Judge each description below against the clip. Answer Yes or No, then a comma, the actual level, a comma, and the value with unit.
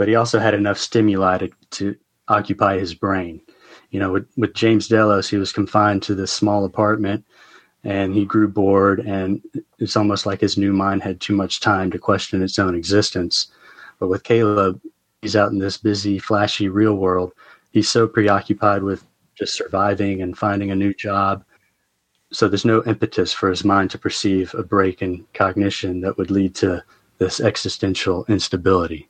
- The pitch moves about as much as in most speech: No, narrow, 1.5 semitones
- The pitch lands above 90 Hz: Yes, low, 100 Hz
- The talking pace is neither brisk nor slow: Yes, average, 175 wpm